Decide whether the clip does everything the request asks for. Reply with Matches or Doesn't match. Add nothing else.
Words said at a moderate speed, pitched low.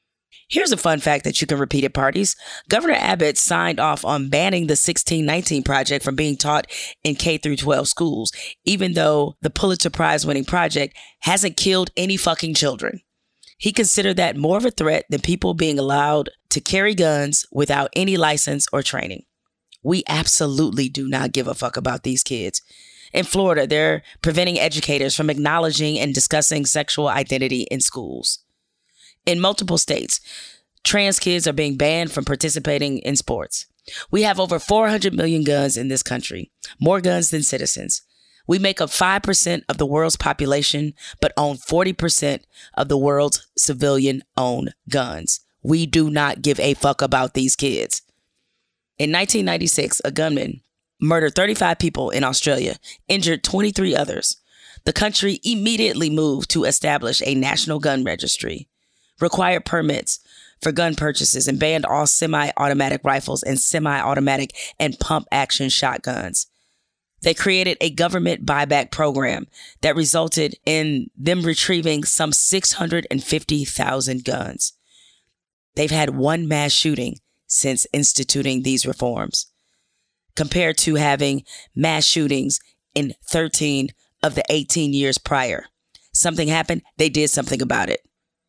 Doesn't match